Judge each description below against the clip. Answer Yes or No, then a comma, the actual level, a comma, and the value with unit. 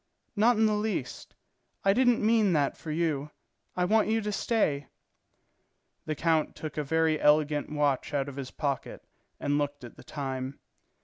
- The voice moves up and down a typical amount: No, wide, 6.5 semitones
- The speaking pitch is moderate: Yes, medium, 155 Hz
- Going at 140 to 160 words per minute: No, average, 170 wpm